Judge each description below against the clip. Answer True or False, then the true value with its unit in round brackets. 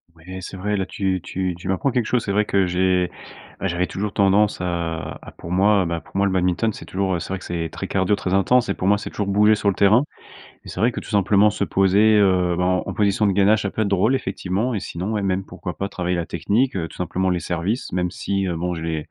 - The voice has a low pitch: True (95 Hz)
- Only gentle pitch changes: True (2.3 semitones)